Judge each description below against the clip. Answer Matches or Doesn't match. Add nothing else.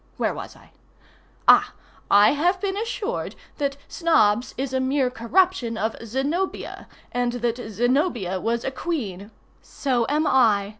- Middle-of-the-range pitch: Doesn't match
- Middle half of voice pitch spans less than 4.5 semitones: Doesn't match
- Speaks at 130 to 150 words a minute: Matches